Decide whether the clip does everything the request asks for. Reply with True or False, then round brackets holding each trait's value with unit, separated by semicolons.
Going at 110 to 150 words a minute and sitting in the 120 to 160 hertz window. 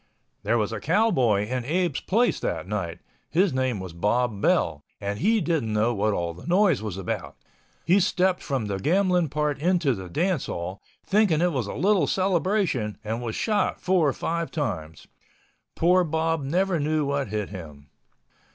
False (175 wpm; 140 Hz)